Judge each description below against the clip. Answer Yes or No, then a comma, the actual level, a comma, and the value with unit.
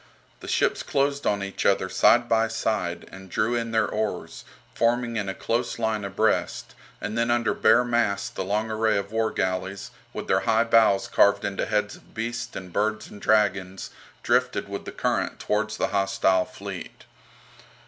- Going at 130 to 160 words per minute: No, average, 170 wpm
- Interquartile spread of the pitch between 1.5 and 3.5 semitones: Yes, narrow, 2.6 semitones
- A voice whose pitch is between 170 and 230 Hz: No, low, 110 Hz